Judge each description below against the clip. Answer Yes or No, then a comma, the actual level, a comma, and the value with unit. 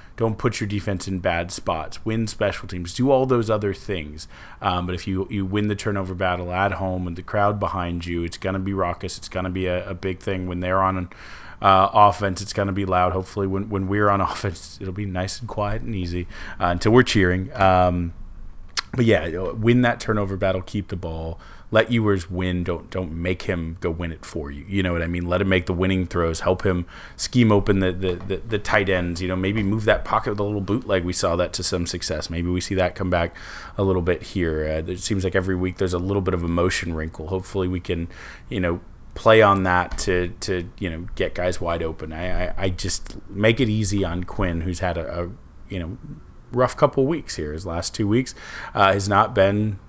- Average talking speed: No, fast, 235 wpm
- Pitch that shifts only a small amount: Yes, narrow, 2.3 semitones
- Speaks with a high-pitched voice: No, very low, 95 Hz